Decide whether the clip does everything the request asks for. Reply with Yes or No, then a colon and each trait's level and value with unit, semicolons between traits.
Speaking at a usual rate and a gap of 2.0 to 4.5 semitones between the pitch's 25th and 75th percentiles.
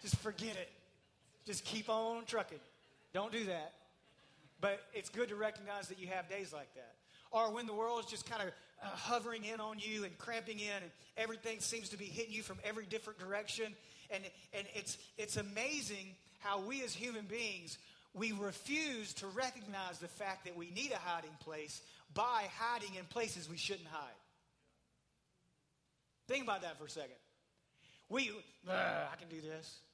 Yes: average, 175 wpm; average, 4.2 semitones